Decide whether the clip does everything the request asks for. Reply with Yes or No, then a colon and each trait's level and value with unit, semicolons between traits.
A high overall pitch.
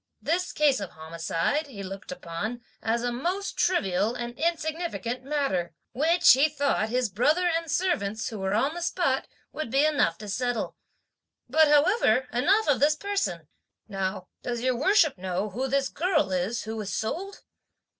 Yes: very high, 255 Hz